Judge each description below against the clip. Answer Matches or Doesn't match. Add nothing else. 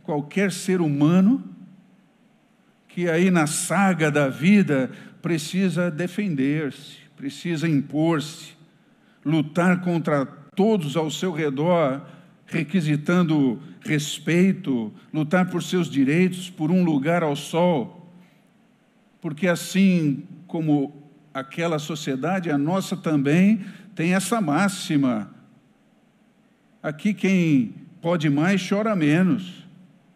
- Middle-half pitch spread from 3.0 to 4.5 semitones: Matches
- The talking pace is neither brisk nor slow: Doesn't match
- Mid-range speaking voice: Matches